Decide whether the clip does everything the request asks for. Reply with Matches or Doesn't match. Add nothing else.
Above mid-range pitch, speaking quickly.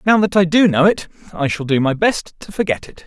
Doesn't match